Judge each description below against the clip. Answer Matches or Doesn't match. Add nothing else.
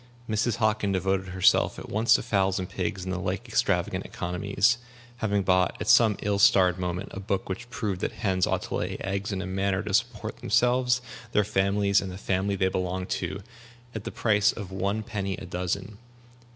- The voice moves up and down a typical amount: Doesn't match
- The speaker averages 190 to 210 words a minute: Matches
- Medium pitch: Doesn't match